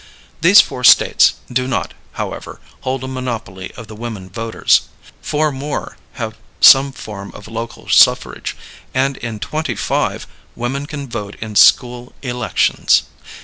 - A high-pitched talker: No, low, 125 Hz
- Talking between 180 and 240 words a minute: No, average, 140 wpm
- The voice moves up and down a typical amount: Yes, average, 3.2 semitones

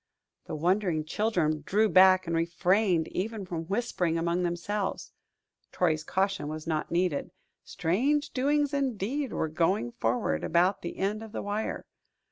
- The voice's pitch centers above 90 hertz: Yes, medium, 185 Hz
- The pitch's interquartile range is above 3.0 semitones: Yes, average, 4.3 semitones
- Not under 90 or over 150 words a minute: Yes, average, 140 wpm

